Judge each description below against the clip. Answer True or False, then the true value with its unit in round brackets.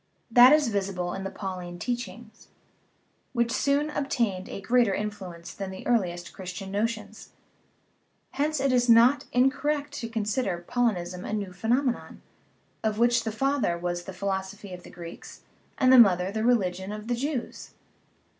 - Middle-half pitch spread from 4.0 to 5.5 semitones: True (4.5 semitones)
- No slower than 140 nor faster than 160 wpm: True (155 wpm)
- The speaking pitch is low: False (215 Hz)